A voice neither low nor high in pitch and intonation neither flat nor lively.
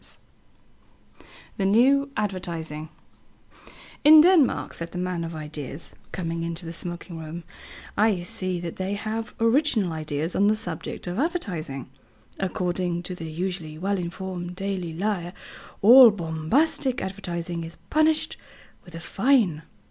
Yes: medium, 180 Hz; average, 4.3 semitones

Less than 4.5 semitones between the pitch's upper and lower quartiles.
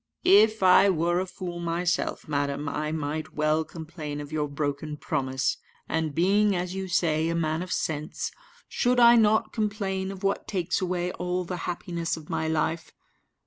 Yes: average, 3.4 semitones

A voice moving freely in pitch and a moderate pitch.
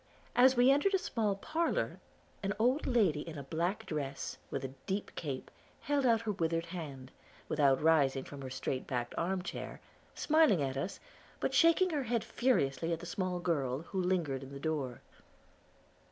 Yes: wide, 8.6 semitones; medium, 170 Hz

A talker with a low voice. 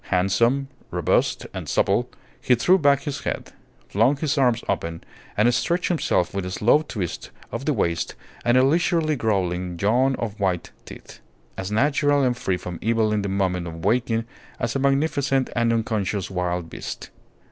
Yes: low, 115 Hz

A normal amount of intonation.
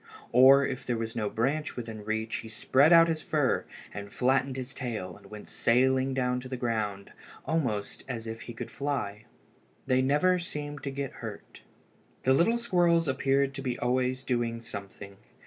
Yes: average, 3.5 semitones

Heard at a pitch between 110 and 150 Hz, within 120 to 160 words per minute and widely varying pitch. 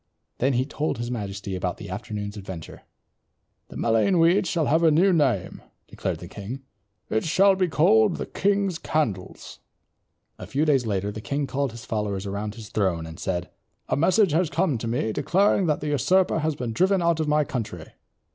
No: low, 135 Hz; average, 195 wpm; wide, 7.7 semitones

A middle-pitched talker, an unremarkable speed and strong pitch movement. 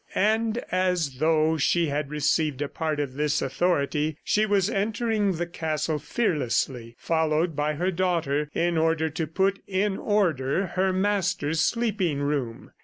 No: medium, 160 Hz; average, 145 wpm; average, 4.2 semitones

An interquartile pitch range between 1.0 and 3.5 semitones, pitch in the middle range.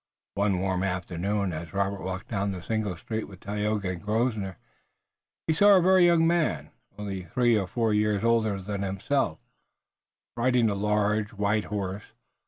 No: average, 2.7 semitones; low, 105 Hz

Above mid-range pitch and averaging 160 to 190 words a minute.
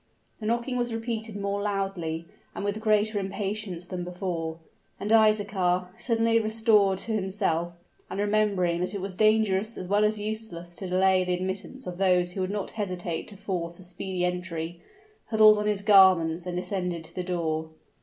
Yes: high, 195 Hz; average, 175 wpm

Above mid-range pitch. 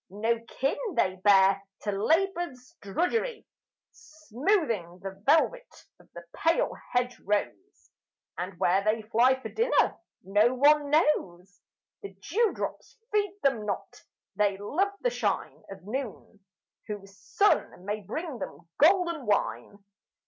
Yes: high, 235 Hz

